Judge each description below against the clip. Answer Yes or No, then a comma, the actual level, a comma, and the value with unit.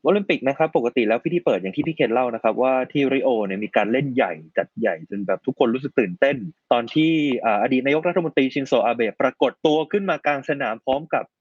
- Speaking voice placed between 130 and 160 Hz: Yes, medium, 140 Hz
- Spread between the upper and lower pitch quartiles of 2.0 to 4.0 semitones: No, average, 4.5 semitones